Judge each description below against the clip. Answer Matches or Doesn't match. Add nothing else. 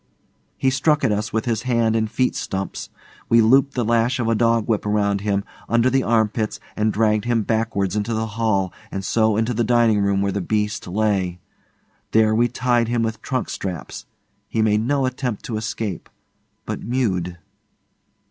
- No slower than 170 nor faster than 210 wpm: Matches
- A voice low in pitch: Matches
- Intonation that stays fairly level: Matches